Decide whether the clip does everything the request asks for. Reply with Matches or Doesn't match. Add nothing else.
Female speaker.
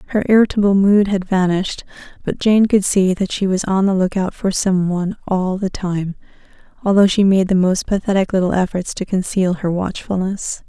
Matches